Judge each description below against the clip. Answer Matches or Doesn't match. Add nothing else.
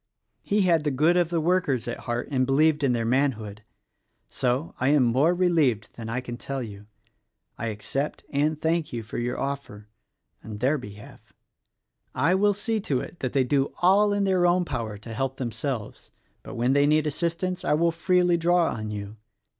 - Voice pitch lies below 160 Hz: Matches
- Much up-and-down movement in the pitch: Matches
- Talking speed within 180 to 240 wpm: Matches